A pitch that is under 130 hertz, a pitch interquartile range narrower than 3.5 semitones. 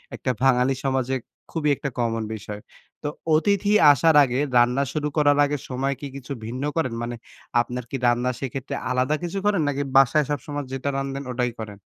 No: low, 135 Hz; average, 2.9 semitones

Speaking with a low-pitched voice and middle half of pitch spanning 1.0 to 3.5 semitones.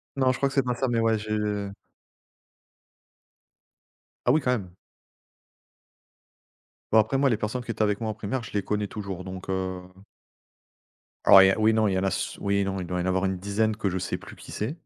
Yes: low, 105 Hz; average, 2.9 semitones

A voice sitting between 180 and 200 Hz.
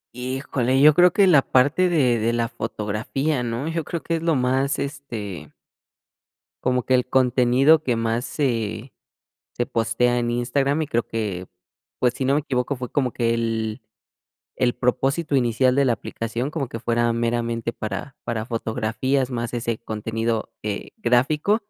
No: low, 125 Hz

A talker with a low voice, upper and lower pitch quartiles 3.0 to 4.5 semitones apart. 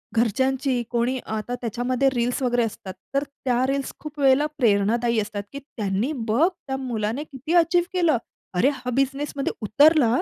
No: very high, 255 Hz; average, 3.3 semitones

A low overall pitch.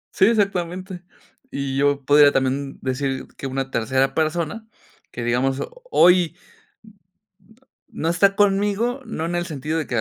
No: medium, 155 Hz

